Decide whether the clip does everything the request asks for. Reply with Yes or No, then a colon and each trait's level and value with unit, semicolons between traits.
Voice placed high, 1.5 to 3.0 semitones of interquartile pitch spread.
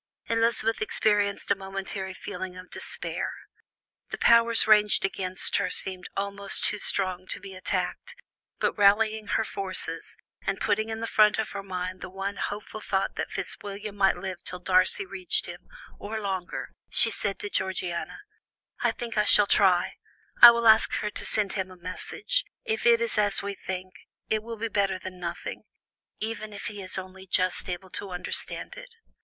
Yes: high, 200 Hz; narrow, 2.6 semitones